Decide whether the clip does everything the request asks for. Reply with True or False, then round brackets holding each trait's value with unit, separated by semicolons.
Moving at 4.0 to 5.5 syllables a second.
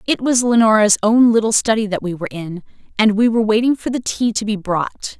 False (5.8 syllables/s)